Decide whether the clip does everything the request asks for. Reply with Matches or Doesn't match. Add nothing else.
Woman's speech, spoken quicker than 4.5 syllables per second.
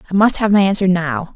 Matches